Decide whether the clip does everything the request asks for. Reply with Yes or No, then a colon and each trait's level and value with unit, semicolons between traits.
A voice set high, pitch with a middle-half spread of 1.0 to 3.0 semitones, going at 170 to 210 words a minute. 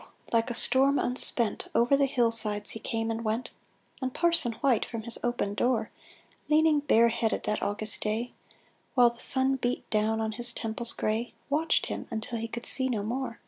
Yes: high, 235 Hz; average, 2.7 semitones; average, 185 wpm